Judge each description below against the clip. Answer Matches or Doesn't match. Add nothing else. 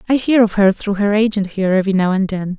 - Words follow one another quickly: Matches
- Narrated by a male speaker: Doesn't match